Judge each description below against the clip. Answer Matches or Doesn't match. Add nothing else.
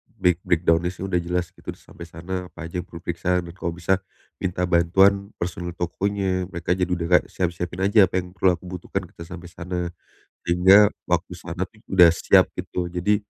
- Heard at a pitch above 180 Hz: Doesn't match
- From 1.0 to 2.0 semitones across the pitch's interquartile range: Matches